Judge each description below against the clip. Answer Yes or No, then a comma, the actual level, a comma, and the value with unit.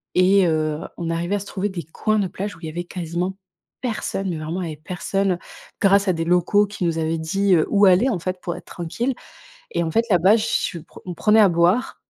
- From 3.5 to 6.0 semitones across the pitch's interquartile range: No, average, 3.0 semitones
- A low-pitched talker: No, medium, 180 Hz